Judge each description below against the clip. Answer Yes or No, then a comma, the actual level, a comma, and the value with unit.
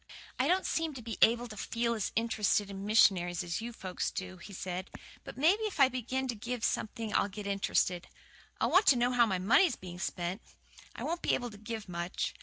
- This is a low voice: No, high, 220 Hz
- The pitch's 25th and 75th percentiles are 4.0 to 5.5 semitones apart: Yes, average, 4.6 semitones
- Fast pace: Yes, fast, 215 wpm